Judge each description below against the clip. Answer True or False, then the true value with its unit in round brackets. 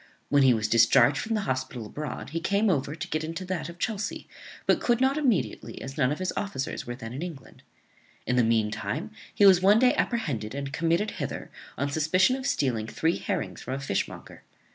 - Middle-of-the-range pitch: True (155 Hz)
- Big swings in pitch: True (7.0 semitones)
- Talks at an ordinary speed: False (210 wpm)